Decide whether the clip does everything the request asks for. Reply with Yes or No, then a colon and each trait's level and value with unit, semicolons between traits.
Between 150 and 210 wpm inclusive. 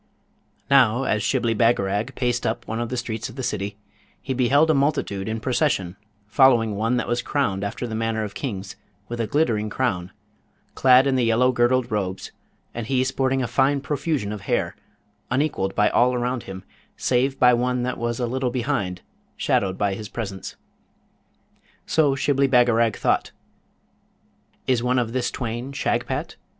Yes: average, 165 wpm